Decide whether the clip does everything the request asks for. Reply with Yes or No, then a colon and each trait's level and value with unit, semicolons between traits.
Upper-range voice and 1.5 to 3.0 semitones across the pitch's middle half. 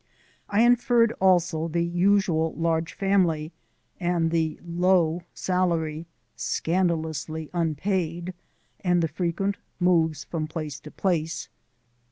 No: medium, 170 Hz; narrow, 2.4 semitones